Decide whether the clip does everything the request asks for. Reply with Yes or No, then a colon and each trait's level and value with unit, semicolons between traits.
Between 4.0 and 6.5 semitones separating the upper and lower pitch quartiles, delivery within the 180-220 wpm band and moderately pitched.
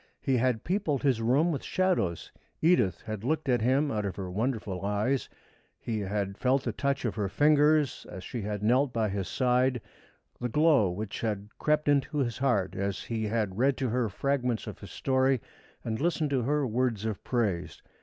No: average, 4.8 semitones; average, 190 wpm; low, 120 Hz